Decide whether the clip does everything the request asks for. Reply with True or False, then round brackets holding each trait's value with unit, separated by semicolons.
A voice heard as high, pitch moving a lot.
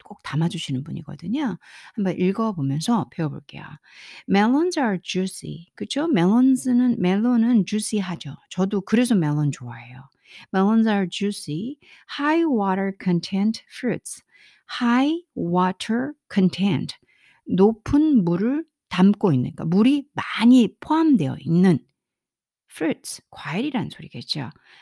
True (200 Hz; 6.1 semitones)